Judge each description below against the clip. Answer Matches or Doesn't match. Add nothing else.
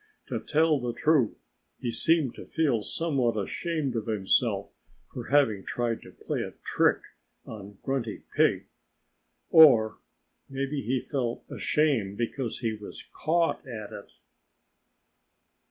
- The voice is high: Doesn't match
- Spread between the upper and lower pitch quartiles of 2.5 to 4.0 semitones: Doesn't match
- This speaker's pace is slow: Matches